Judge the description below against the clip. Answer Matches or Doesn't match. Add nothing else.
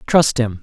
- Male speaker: Matches